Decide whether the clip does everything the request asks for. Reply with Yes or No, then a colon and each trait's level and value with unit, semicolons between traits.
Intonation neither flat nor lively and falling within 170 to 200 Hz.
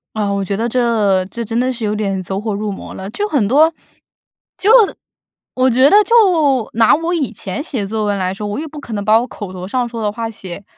No: average, 4.1 semitones; high, 220 Hz